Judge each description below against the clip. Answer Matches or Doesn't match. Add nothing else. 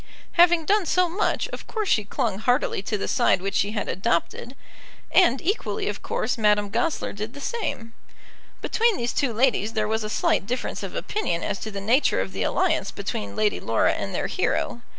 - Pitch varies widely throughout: Matches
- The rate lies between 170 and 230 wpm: Matches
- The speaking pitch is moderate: Doesn't match